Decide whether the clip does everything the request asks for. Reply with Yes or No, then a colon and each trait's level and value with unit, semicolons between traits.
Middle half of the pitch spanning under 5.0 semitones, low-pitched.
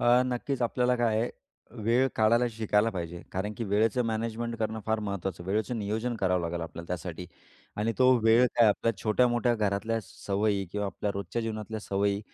Yes: average, 2.9 semitones; low, 110 Hz